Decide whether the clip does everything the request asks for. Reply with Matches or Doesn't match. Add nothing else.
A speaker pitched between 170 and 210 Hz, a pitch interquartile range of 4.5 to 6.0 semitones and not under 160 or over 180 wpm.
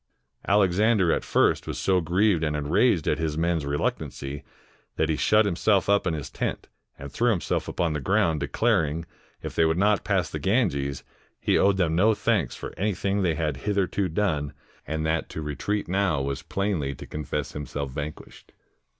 Doesn't match